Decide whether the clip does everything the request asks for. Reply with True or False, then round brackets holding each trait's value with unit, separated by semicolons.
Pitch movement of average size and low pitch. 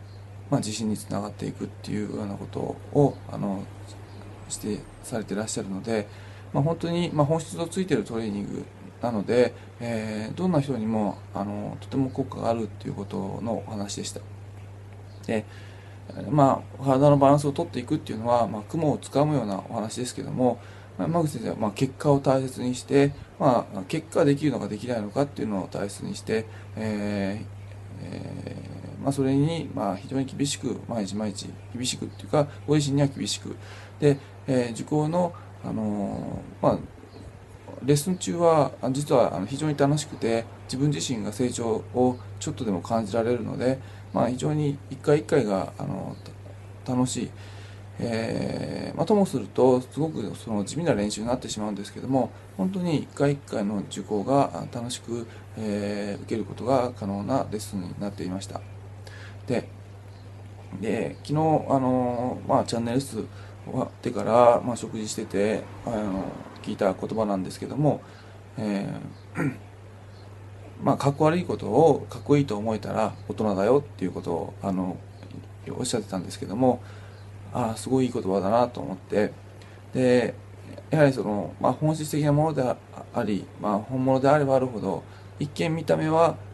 True (4.8 semitones; 105 Hz)